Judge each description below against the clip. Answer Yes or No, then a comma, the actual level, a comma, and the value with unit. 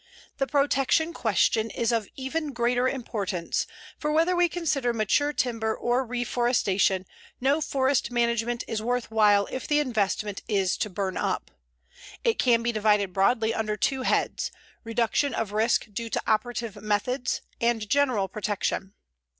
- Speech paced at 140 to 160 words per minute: Yes, average, 145 wpm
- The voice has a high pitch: Yes, high, 235 Hz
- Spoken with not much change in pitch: No, average, 3.7 semitones